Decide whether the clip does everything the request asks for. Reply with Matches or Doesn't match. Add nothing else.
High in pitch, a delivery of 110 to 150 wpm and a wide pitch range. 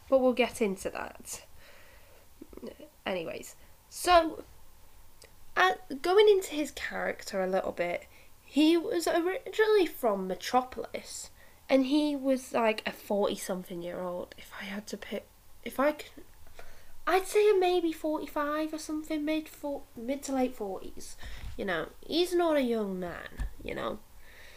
Matches